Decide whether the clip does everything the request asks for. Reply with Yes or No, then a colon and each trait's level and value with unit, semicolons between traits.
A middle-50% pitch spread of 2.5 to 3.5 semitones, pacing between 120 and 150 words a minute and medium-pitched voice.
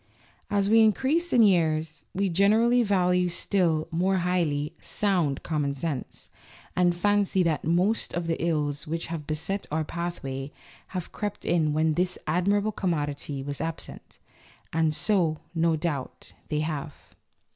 No: average, 4.0 semitones; average, 140 wpm; medium, 170 Hz